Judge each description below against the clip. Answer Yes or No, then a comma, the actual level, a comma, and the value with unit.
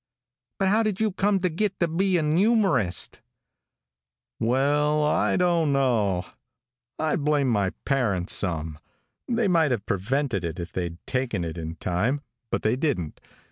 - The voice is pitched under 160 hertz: Yes, low, 135 Hz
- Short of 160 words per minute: Yes, average, 150 wpm